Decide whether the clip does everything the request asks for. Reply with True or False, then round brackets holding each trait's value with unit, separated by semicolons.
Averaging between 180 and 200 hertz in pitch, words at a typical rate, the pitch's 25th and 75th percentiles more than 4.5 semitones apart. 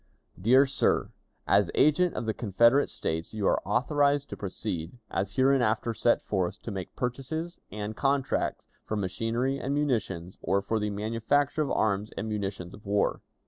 False (110 Hz; 160 wpm; 5.2 semitones)